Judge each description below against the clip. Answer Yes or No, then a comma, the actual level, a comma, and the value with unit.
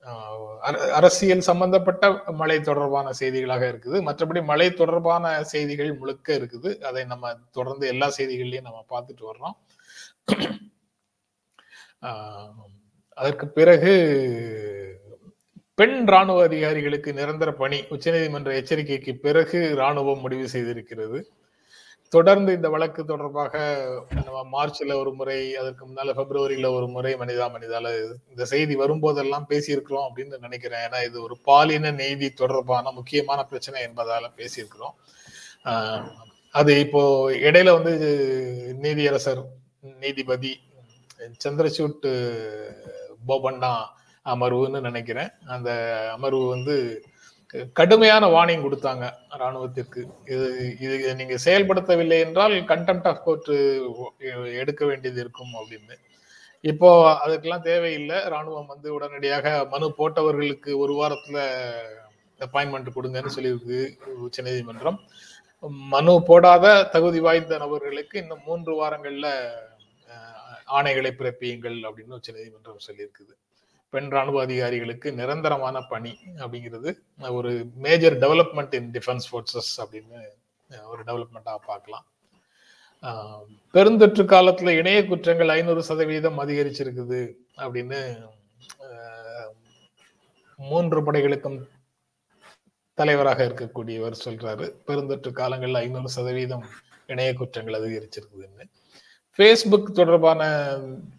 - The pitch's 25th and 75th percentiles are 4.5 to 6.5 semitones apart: No, average, 4.1 semitones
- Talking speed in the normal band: Yes, average, 95 wpm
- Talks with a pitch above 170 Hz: No, low, 135 Hz